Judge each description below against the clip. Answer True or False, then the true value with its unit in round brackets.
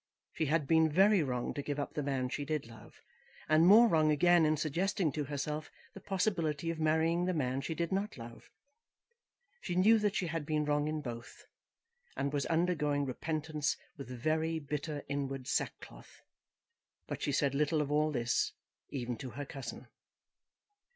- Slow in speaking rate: False (170 wpm)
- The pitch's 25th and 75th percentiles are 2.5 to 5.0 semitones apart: True (2.8 semitones)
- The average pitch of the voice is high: False (150 Hz)